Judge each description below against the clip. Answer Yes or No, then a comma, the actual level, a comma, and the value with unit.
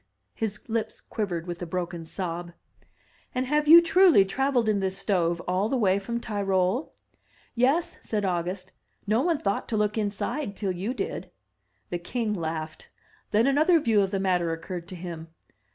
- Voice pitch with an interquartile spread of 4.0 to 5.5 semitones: Yes, average, 4.9 semitones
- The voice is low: No, high, 200 Hz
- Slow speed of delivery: No, average, 170 wpm